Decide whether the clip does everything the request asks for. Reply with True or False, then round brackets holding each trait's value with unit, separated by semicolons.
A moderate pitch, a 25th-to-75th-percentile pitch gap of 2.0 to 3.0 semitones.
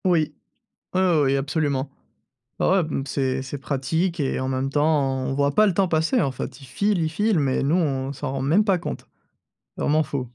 False (145 Hz; 4.0 semitones)